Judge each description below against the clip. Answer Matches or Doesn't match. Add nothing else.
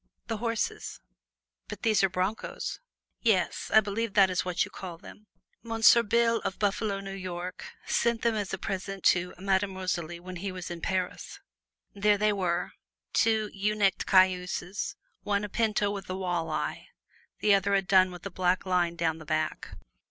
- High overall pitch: Matches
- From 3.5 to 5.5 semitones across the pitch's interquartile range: Doesn't match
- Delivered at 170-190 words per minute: Matches